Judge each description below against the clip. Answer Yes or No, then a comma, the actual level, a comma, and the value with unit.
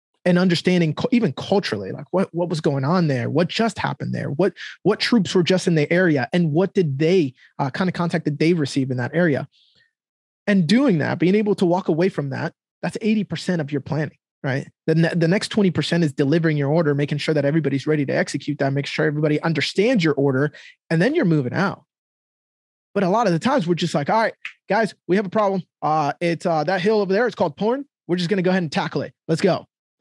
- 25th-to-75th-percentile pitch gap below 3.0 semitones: No, average, 4.2 semitones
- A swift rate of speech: Yes, fast, 240 wpm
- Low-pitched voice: No, medium, 170 Hz